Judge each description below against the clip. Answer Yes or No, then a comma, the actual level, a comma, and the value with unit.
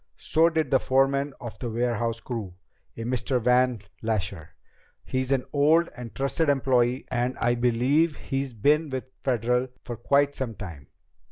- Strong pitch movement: No, average, 2.9 semitones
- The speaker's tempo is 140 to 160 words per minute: Yes, average, 155 wpm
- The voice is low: Yes, low, 125 Hz